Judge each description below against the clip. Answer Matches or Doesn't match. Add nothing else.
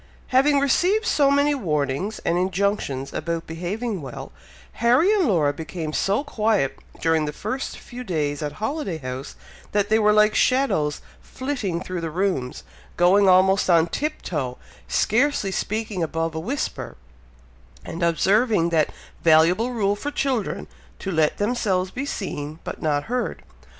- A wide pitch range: Matches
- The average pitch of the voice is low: Doesn't match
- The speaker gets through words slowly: Doesn't match